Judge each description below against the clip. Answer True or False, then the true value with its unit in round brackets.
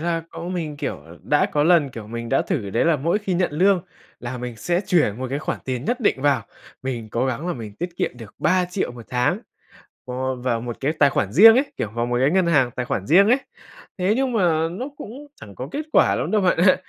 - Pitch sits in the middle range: True (150 Hz)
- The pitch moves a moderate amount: False (6.6 semitones)